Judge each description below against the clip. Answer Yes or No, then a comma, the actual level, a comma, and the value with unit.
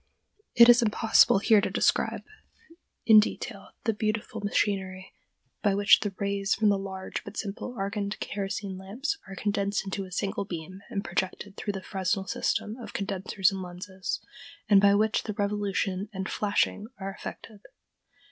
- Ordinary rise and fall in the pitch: No, narrow, 1.6 semitones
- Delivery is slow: No, average, 155 wpm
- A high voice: Yes, high, 200 Hz